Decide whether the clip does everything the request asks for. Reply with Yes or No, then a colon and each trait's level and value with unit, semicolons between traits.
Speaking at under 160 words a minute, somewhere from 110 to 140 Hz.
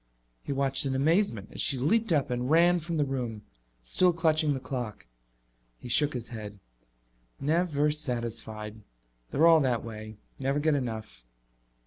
Yes: average, 150 wpm; low, 135 Hz